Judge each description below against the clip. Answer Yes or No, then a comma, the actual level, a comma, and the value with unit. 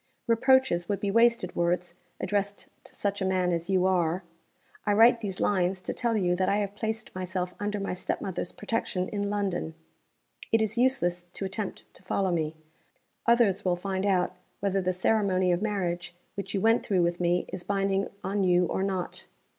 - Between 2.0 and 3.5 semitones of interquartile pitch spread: Yes, narrow, 2.5 semitones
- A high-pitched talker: Yes, high, 195 Hz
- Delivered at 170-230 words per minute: Yes, average, 185 wpm